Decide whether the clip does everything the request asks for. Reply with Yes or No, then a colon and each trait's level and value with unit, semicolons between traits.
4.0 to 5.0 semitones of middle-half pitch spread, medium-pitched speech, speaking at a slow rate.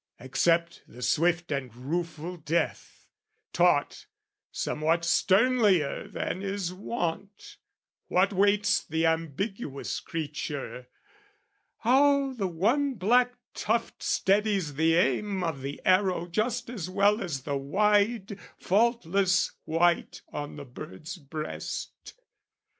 Yes: average, 4.7 semitones; medium, 180 Hz; slow, 105 wpm